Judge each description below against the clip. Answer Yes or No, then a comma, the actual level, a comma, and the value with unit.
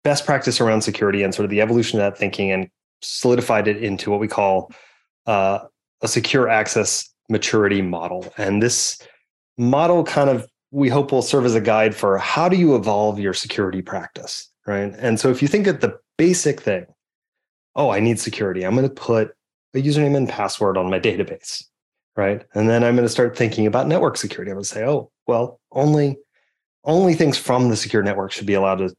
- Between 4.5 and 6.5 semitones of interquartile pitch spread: Yes, average, 5.0 semitones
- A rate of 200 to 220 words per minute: Yes, fast, 205 wpm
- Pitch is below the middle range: Yes, low, 115 Hz